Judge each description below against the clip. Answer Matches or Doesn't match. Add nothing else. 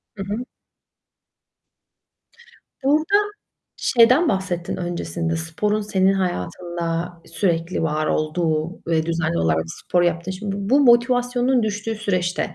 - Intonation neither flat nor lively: Matches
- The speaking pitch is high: Doesn't match